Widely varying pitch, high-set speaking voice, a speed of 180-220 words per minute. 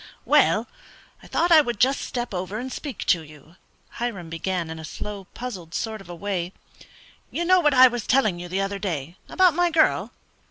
Yes: wide, 6.8 semitones; high, 205 Hz; average, 200 wpm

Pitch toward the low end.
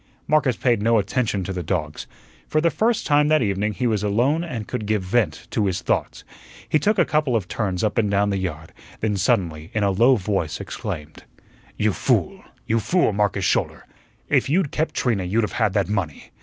Yes: low, 105 Hz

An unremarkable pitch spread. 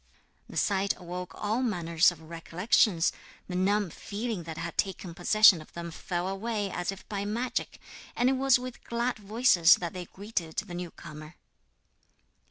Yes: average, 3.9 semitones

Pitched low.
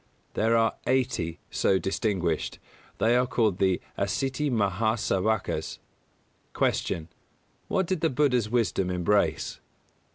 Yes: low, 110 Hz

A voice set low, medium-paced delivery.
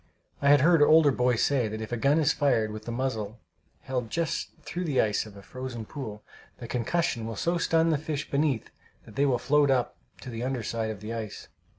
No: low, 130 Hz; fast, 225 wpm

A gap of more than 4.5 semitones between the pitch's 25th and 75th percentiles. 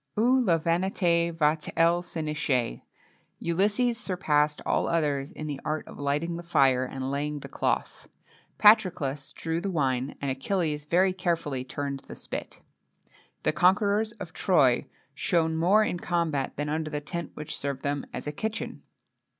No: average, 3.9 semitones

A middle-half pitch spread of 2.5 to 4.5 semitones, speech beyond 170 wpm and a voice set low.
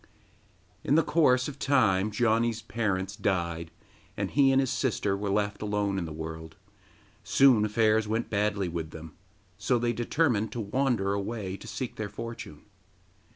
No: average, 3.5 semitones; average, 155 wpm; low, 105 Hz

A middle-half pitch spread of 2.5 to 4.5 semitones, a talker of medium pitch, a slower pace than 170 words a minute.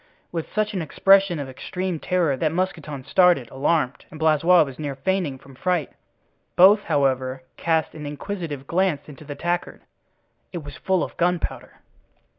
Yes: average, 4.2 semitones; medium, 160 Hz; average, 150 wpm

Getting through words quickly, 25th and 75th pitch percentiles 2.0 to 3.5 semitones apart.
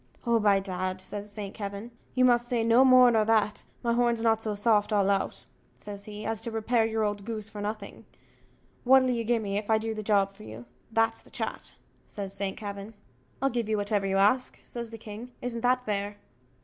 Yes: fast, 210 wpm; narrow, 2.4 semitones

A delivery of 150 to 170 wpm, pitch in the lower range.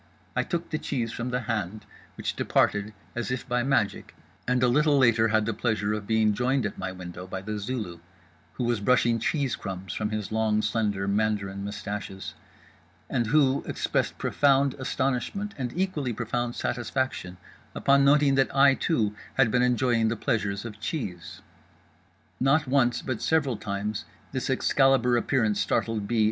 Yes: average, 160 wpm; low, 115 Hz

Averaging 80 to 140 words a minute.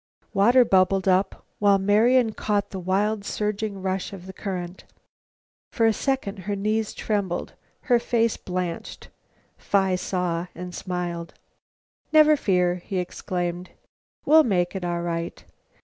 Yes: slow, 135 wpm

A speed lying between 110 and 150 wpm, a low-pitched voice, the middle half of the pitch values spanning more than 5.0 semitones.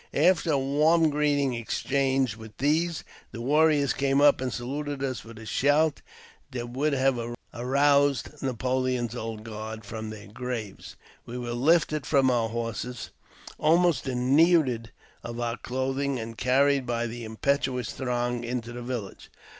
No: average, 145 wpm; low, 130 Hz; average, 3.2 semitones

